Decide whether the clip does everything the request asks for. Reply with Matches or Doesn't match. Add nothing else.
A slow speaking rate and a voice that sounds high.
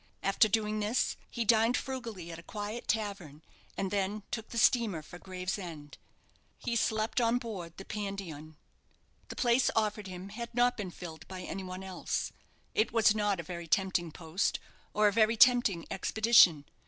Doesn't match